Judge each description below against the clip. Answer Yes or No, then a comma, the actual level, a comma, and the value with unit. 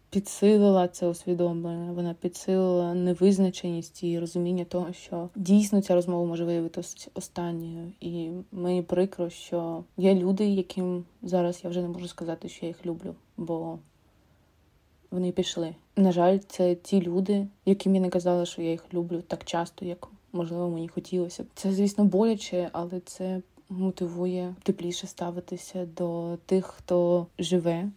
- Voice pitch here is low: No, medium, 180 Hz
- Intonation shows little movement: Yes, narrow, 1.5 semitones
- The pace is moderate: Yes, average, 145 wpm